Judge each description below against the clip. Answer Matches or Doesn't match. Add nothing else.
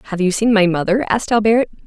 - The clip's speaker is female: Matches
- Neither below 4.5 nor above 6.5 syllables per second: Doesn't match